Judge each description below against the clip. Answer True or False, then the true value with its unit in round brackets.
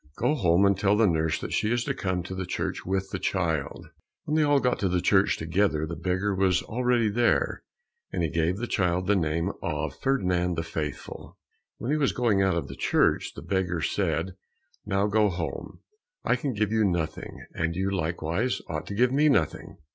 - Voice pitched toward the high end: False (95 Hz)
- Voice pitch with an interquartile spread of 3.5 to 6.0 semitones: True (4.3 semitones)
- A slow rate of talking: False (205 wpm)